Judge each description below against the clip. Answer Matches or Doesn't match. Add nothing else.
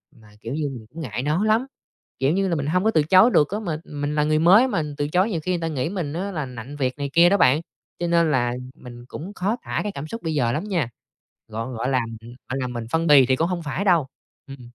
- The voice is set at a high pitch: Doesn't match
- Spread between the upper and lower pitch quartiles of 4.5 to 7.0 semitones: Matches